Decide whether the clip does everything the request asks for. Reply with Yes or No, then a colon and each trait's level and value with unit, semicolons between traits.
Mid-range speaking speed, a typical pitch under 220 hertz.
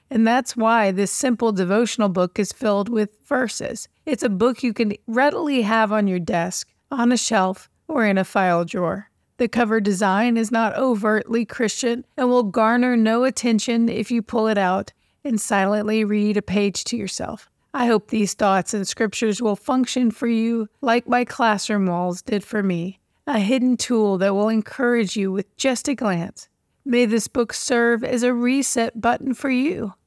No: average, 180 wpm; high, 225 Hz